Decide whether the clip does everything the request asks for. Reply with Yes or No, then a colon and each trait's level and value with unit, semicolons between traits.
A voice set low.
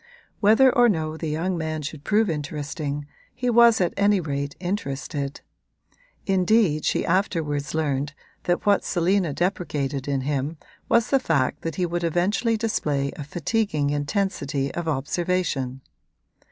No: medium, 160 Hz